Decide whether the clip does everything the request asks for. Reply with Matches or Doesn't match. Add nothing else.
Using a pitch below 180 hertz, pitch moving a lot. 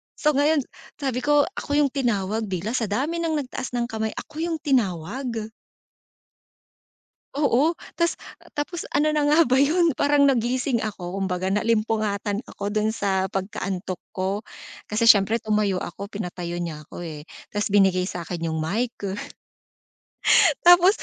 Doesn't match